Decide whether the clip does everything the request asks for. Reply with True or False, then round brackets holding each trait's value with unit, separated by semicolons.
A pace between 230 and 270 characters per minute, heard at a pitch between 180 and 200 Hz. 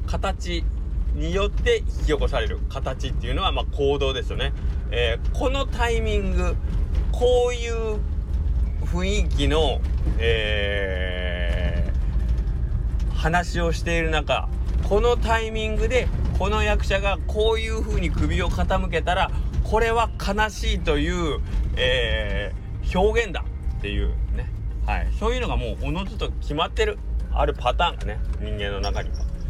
False (265 characters per minute; 75 Hz)